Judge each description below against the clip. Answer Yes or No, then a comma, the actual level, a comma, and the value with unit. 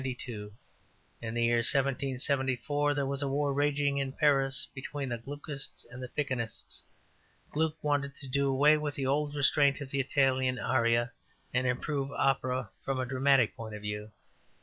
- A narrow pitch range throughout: Yes, narrow, 2.0 semitones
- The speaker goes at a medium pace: Yes, average, 150 wpm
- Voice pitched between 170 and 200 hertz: No, low, 135 Hz